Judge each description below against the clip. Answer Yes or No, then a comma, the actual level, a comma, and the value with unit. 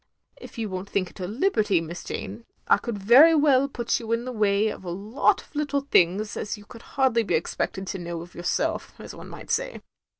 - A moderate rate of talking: No, fast, 225 wpm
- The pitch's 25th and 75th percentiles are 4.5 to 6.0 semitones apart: Yes, wide, 5.6 semitones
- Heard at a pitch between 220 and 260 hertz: No, high, 210 Hz